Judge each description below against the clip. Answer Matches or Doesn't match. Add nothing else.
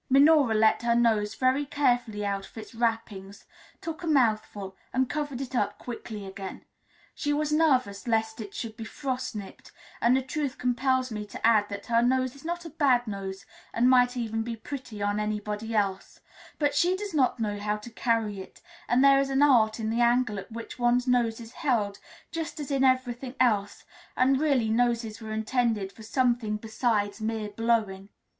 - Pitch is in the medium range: Doesn't match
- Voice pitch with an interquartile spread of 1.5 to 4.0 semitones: Matches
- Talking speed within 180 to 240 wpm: Matches